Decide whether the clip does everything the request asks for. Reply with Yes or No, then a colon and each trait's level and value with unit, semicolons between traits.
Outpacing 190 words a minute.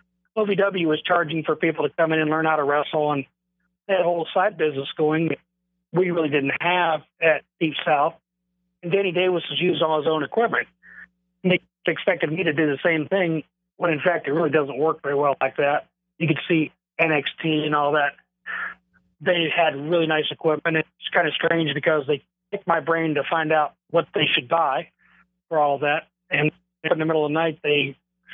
Yes: fast, 205 wpm